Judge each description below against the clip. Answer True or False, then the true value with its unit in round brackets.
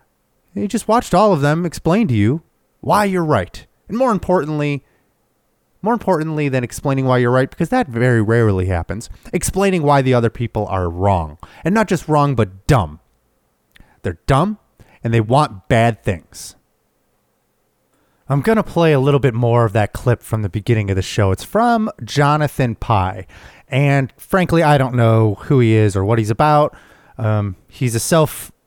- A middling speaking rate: True (175 wpm)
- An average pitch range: False (6.7 semitones)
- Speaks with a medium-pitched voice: False (125 Hz)